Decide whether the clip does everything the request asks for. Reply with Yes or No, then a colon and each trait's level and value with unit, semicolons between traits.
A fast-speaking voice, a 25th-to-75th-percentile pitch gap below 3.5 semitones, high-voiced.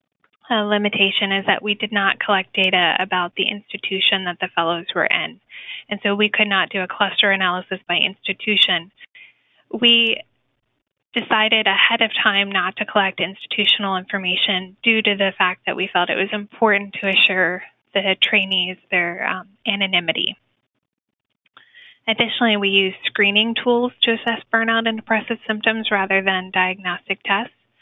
No: average, 150 wpm; average, 2.8 semitones; high, 200 Hz